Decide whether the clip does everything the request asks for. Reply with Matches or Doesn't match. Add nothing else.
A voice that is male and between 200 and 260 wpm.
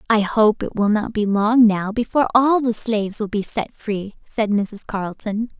Doesn't match